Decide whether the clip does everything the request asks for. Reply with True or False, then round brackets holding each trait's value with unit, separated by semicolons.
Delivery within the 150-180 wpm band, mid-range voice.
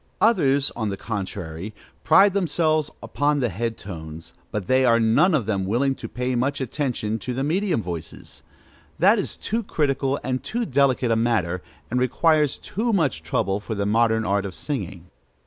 False (175 wpm; 125 Hz)